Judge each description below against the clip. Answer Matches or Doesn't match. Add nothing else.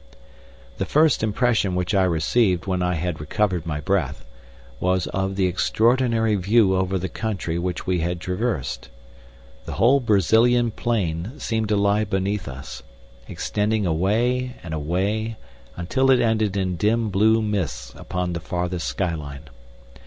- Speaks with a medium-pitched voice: Doesn't match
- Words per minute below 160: Matches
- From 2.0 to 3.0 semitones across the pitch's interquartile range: Doesn't match